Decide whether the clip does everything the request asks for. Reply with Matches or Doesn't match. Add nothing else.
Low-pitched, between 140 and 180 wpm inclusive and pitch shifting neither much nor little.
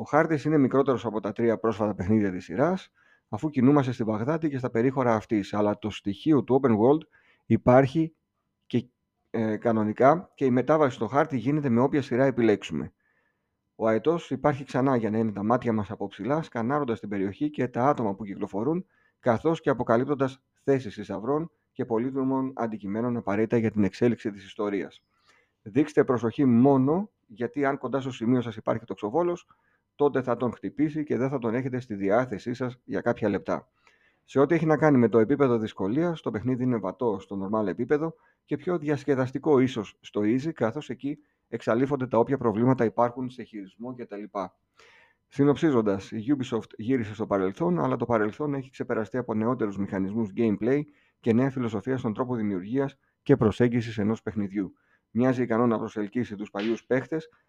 Matches